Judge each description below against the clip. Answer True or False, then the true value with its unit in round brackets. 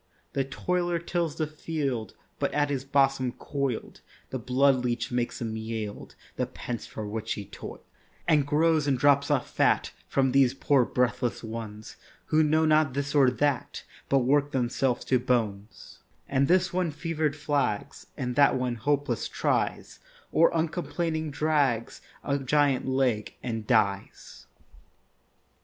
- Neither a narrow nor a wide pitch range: True (3.4 semitones)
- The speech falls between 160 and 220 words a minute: False (145 wpm)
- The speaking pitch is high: False (135 Hz)